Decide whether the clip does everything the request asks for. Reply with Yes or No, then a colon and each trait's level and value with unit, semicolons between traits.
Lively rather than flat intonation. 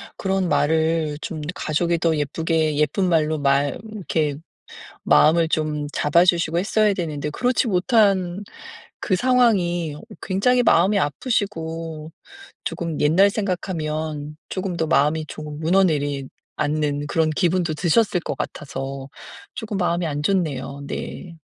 No: average, 3.7 semitones